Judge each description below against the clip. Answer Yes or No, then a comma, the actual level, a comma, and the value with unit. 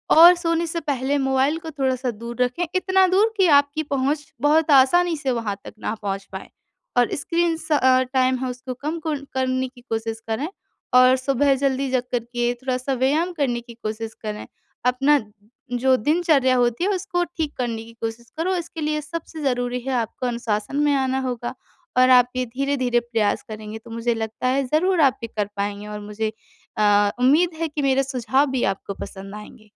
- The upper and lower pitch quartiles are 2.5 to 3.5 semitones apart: No, average, 4.1 semitones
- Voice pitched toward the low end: No, very high, 260 Hz